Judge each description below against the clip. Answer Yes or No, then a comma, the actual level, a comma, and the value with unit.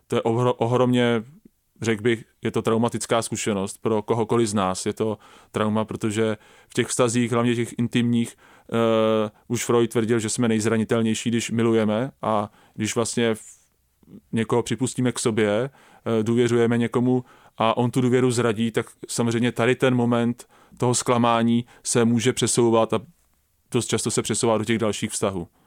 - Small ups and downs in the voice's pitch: Yes, narrow, 1.5 semitones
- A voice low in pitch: Yes, low, 115 Hz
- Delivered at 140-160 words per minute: Yes, average, 155 wpm